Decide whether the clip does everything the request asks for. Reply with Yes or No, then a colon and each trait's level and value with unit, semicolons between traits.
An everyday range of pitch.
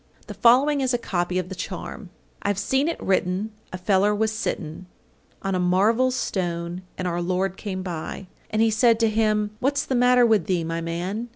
Yes: average, 3.9 semitones